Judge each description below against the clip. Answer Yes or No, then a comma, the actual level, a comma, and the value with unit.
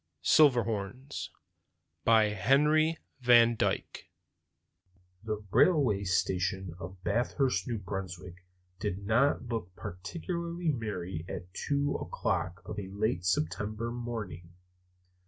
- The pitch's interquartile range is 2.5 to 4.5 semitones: No, average, 5.0 semitones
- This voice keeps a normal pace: No, slow, 100 wpm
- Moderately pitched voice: No, low, 105 Hz